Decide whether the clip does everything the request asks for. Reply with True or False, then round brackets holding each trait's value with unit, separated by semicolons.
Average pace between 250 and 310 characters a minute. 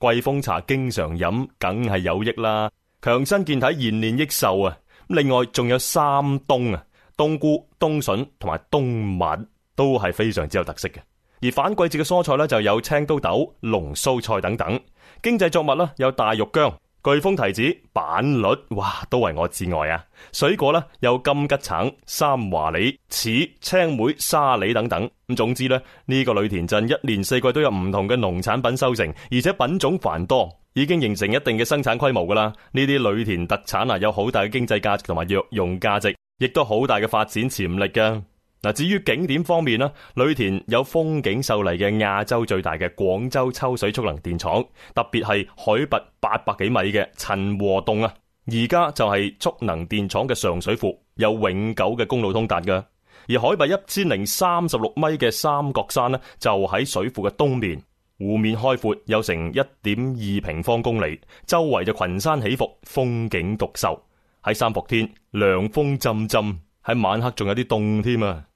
True (265 characters per minute)